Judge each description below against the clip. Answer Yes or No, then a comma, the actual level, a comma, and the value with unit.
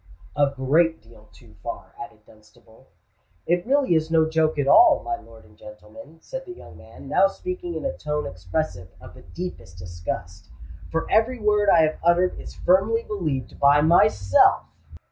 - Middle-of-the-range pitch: Yes, medium, 160 Hz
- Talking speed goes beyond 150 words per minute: Yes, average, 170 wpm